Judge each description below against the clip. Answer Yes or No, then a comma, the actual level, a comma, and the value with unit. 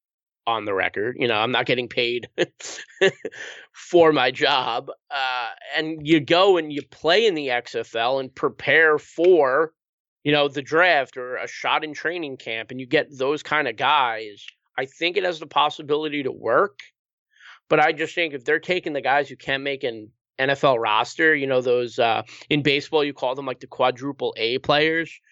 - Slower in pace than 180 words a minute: No, average, 185 wpm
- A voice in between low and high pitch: Yes, medium, 150 Hz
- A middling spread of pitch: Yes, average, 3.6 semitones